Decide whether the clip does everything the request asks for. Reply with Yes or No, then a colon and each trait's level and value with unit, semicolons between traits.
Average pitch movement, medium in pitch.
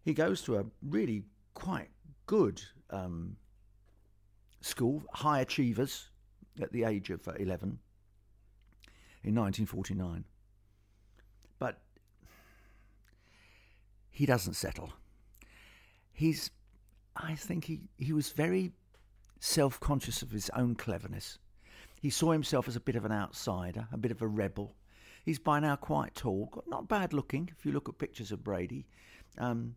No: average, 4.5 semitones; low, 105 Hz